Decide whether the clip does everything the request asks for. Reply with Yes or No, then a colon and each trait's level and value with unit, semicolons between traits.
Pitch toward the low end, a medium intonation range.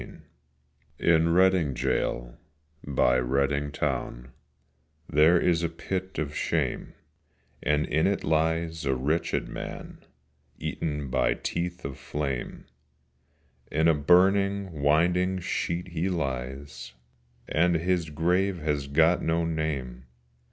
Yes: very low, 80 Hz; average, 3.7 semitones